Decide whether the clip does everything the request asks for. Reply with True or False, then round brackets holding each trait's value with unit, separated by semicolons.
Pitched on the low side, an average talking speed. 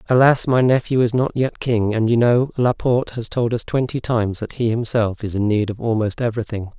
False (115 Hz; 220 wpm)